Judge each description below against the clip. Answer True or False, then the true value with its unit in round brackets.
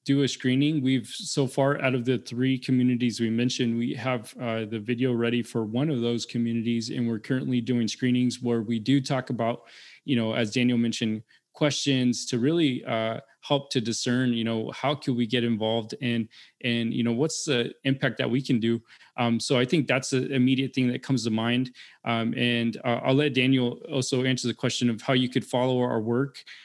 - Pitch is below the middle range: True (125 Hz)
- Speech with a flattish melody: True (2.0 semitones)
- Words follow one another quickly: True (210 wpm)